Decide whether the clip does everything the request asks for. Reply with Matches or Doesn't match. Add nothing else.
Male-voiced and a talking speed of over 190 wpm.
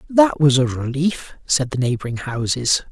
Doesn't match